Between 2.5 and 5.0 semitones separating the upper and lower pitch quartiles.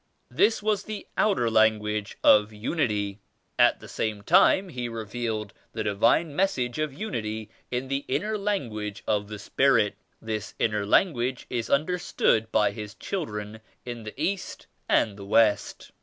No: wide, 5.6 semitones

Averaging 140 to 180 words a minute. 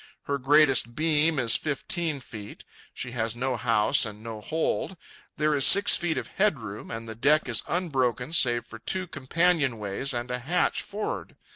Yes: average, 165 wpm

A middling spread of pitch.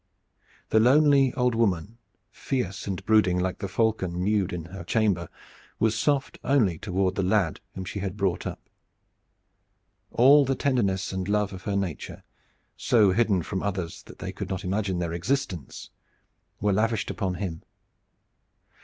Yes: average, 3.5 semitones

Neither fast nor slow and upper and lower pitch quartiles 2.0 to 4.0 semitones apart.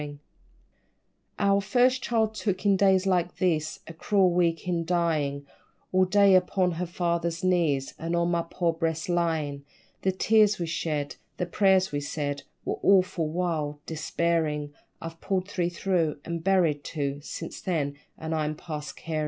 Yes: average, 160 wpm; average, 3.1 semitones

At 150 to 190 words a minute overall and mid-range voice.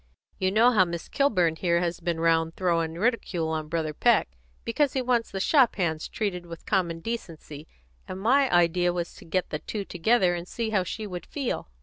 No: average, 200 wpm; medium, 180 Hz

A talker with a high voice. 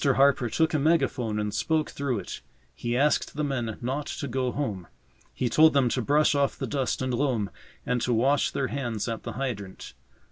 No: low, 130 Hz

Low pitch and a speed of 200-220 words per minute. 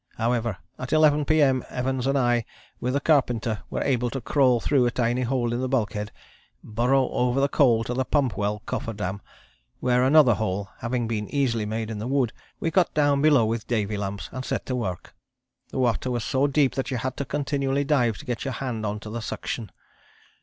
Yes: low, 125 Hz; fast, 205 wpm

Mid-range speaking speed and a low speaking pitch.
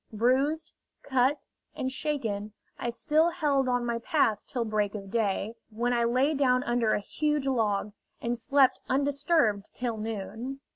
No: average, 150 wpm; high, 245 Hz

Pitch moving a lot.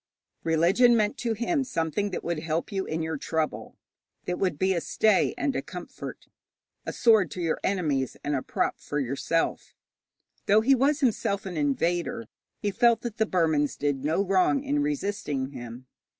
Yes: wide, 6.4 semitones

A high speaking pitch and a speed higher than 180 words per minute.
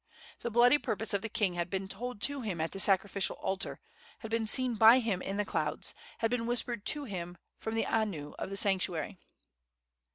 Yes: high, 210 Hz; average, 200 wpm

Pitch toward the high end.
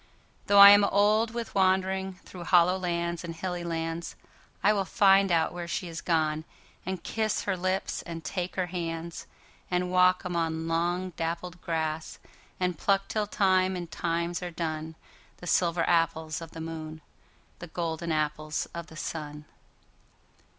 No: medium, 175 Hz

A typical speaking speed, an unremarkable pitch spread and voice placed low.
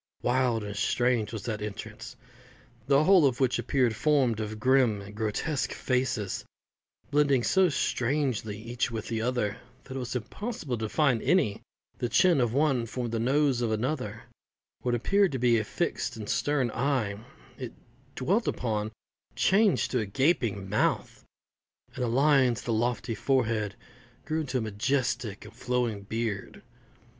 Yes: average, 155 wpm; average, 3.8 semitones; low, 120 Hz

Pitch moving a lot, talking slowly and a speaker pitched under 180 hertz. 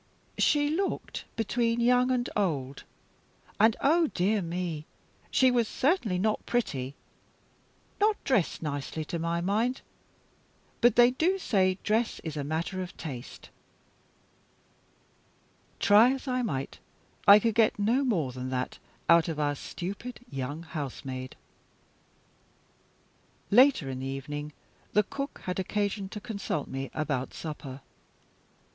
No: wide, 8.3 semitones; slow, 125 wpm; high, 190 Hz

